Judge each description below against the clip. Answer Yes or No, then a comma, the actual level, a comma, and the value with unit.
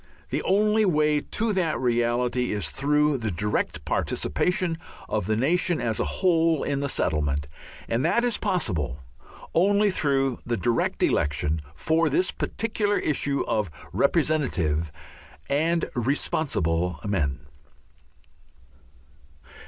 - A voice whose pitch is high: No, medium, 140 Hz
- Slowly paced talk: Yes, slow, 115 wpm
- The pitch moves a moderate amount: No, wide, 8.6 semitones